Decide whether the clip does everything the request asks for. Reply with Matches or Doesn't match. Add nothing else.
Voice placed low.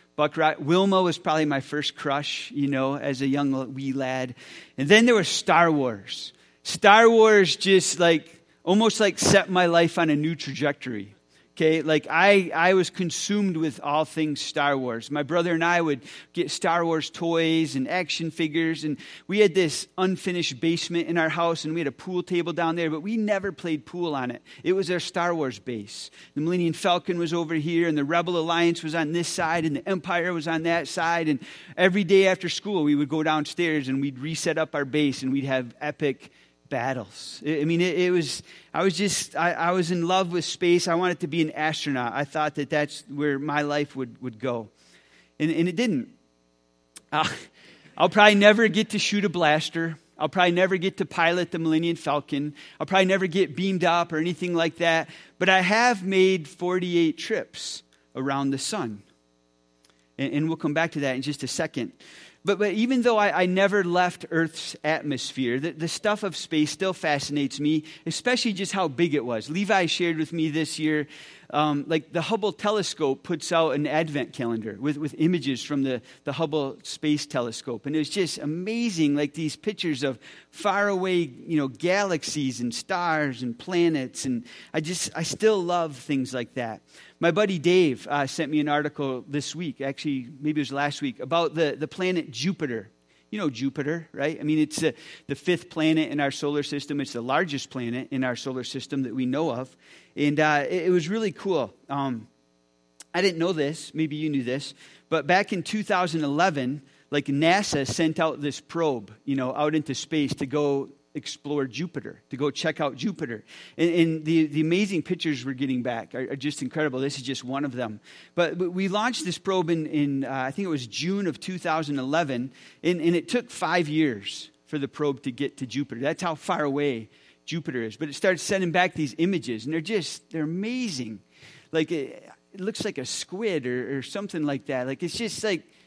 Doesn't match